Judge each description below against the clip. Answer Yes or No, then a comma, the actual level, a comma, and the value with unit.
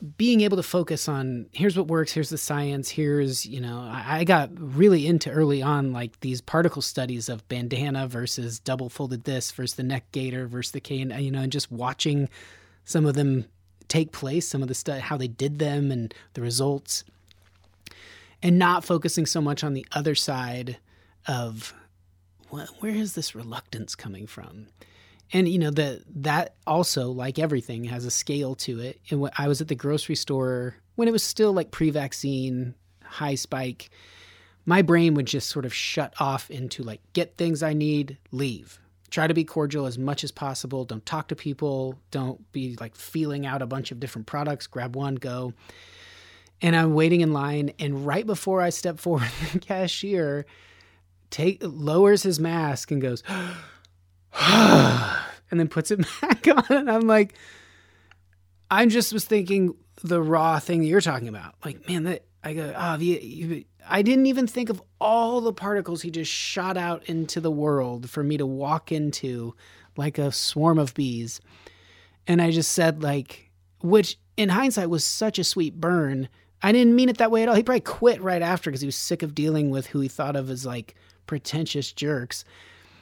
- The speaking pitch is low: No, medium, 145 Hz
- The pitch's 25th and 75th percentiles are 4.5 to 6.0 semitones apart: Yes, average, 5.3 semitones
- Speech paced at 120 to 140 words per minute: No, average, 190 wpm